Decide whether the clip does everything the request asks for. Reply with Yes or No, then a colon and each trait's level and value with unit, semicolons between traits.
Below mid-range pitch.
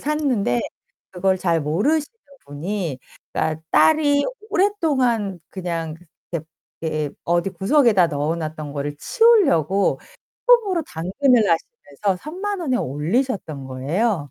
No: high, 190 Hz